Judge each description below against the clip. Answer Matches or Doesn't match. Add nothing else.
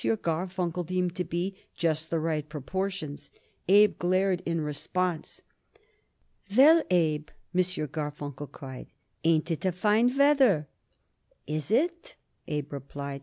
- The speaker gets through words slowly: Matches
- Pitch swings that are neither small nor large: Matches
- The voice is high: Doesn't match